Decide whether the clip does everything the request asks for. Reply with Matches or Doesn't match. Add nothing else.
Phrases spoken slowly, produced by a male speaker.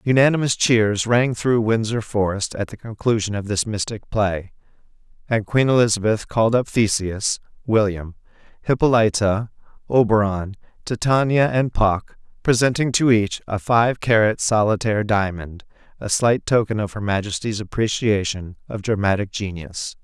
Matches